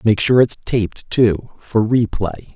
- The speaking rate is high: No, average, 165 wpm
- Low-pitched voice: Yes, low, 110 Hz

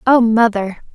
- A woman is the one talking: Yes, female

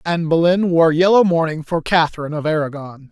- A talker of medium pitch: Yes, medium, 165 Hz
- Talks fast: No, average, 175 wpm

